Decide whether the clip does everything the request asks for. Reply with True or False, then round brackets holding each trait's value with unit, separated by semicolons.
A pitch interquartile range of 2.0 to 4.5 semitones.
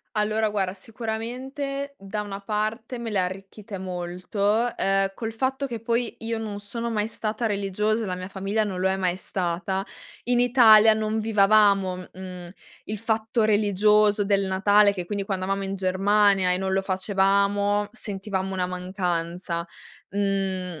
True (2.4 semitones)